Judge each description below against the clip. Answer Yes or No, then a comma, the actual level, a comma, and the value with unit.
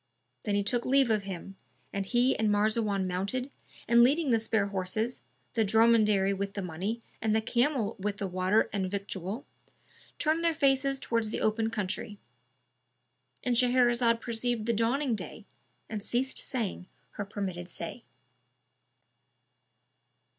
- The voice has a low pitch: No, high, 215 Hz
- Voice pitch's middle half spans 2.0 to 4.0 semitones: Yes, average, 3.6 semitones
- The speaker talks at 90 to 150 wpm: Yes, average, 140 wpm